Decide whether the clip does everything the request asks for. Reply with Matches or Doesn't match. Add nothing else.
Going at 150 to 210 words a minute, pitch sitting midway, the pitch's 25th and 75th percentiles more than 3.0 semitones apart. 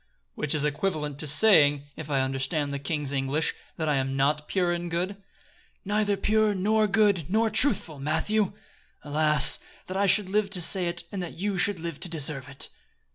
Matches